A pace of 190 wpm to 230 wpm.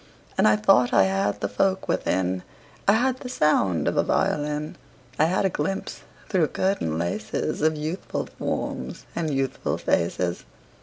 No: average, 155 wpm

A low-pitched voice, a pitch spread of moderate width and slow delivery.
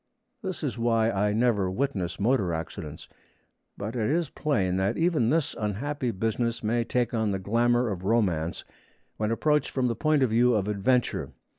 No: low, 115 Hz; average, 4.1 semitones; average, 170 wpm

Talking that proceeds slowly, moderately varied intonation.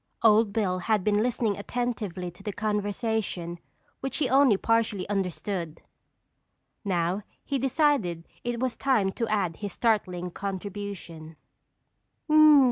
Yes: slow, 120 wpm; average, 4.0 semitones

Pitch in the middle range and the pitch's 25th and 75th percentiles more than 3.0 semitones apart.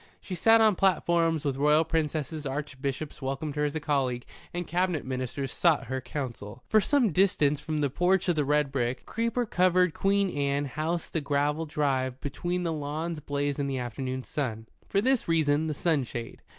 Yes: medium, 150 Hz; average, 3.9 semitones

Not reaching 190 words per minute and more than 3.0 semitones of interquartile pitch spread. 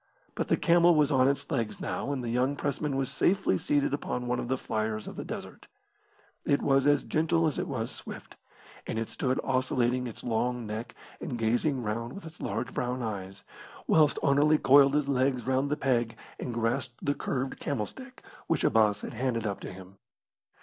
No: average, 195 wpm; average, 3.6 semitones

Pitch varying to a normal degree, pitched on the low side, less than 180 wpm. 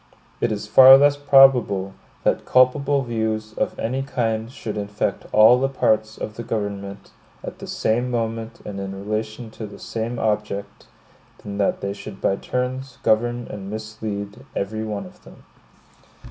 Yes: average, 3.0 semitones; low, 110 Hz; average, 160 wpm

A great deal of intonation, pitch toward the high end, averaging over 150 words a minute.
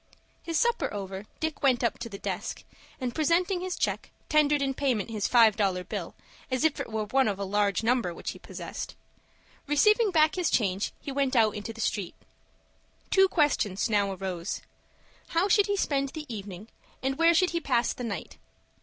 Yes: wide, 7.2 semitones; very high, 250 Hz; average, 190 wpm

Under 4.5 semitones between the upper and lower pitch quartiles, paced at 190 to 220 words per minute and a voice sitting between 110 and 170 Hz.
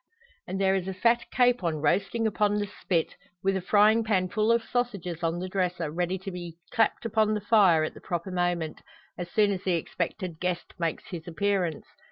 No: average, 3.3 semitones; average, 200 wpm; medium, 185 Hz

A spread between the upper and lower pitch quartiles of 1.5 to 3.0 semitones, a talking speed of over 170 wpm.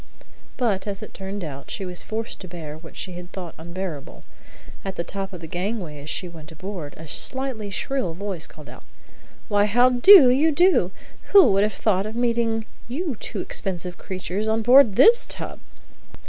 No: average, 5.0 semitones; average, 190 wpm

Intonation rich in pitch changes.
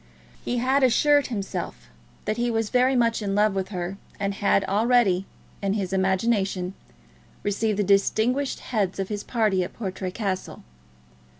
No: average, 3.5 semitones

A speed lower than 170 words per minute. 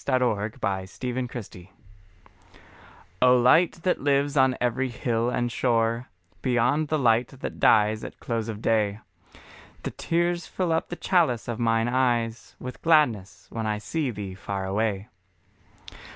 Yes: average, 145 wpm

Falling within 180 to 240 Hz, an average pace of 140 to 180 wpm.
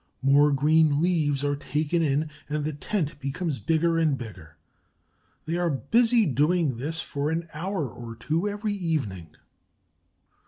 No: medium, 150 Hz; average, 145 wpm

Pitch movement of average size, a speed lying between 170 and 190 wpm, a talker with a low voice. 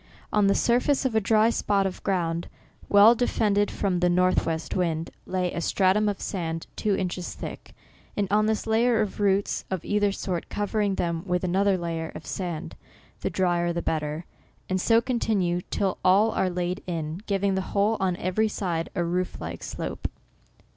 No: average, 3.0 semitones; average, 180 wpm; high, 190 Hz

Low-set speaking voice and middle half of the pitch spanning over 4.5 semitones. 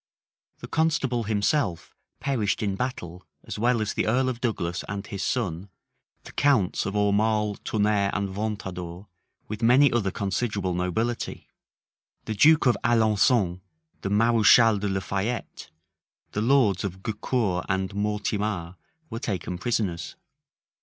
No: low, 105 Hz; average, 3.4 semitones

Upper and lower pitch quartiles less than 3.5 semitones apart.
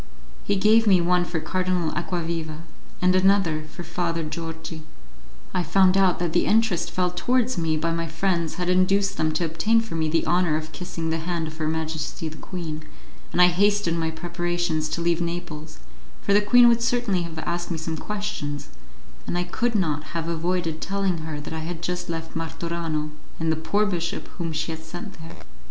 Yes: narrow, 2.4 semitones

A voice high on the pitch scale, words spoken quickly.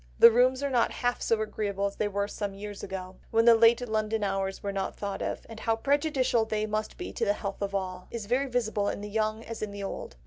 Yes: high, 215 Hz; fast, 250 wpm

